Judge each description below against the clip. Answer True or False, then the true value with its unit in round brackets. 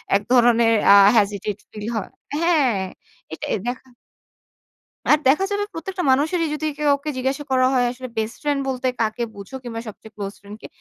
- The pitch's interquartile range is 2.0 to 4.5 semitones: False (5.2 semitones)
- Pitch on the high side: True (255 Hz)